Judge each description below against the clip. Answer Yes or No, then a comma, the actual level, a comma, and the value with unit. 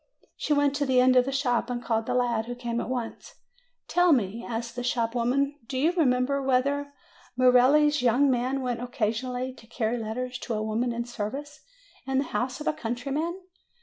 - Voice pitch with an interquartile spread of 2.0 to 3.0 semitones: Yes, narrow, 2.6 semitones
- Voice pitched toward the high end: Yes, very high, 250 Hz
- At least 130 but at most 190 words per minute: No, average, 200 wpm